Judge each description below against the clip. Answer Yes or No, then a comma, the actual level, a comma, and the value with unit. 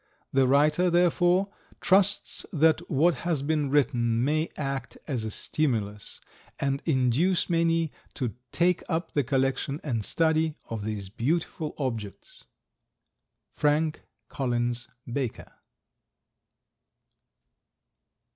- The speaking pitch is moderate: Yes, medium, 145 Hz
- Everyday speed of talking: No, slow, 100 wpm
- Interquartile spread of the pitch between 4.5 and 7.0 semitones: Yes, average, 4.9 semitones